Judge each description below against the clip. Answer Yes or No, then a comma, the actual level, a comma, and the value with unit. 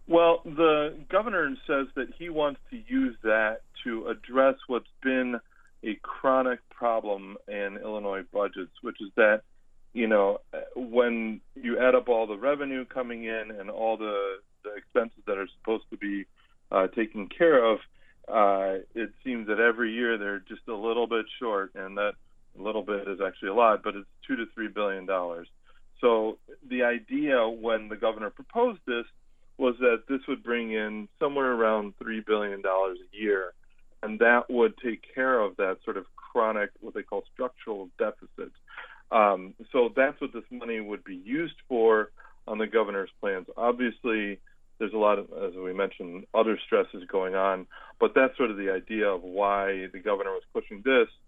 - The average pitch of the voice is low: Yes, low, 115 Hz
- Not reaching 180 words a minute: Yes, average, 170 wpm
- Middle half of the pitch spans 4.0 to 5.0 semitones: Yes, average, 4.4 semitones